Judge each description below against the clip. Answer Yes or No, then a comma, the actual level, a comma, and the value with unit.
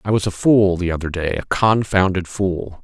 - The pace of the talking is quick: No, average, 190 wpm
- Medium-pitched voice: No, very low, 95 Hz